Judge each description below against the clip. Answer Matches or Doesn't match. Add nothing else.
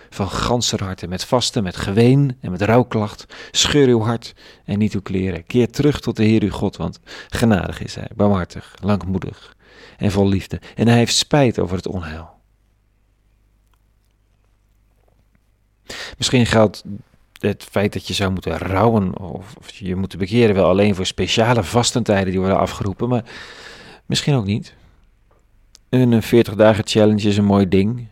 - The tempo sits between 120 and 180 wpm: Matches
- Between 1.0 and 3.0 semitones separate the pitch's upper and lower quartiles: Matches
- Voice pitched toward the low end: Matches